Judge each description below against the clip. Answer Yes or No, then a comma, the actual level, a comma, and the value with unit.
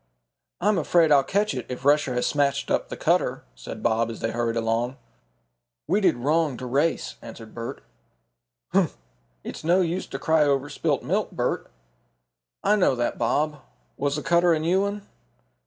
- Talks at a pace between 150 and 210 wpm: Yes, average, 170 wpm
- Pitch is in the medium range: Yes, medium, 145 Hz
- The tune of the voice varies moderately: No, wide, 5.7 semitones